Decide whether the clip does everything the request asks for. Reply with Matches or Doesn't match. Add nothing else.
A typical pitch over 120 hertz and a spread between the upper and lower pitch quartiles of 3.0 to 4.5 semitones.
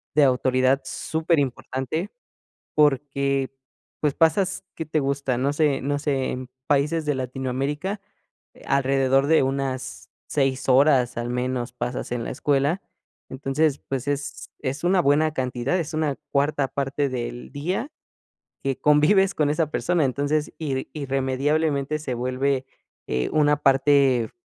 Doesn't match